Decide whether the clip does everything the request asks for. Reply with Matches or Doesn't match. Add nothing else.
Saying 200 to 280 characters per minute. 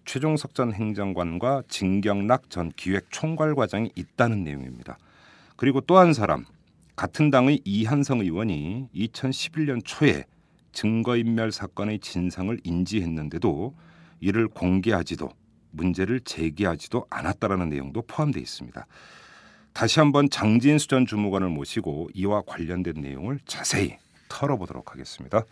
Doesn't match